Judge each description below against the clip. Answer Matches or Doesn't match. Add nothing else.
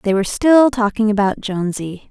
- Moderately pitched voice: Doesn't match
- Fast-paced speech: Doesn't match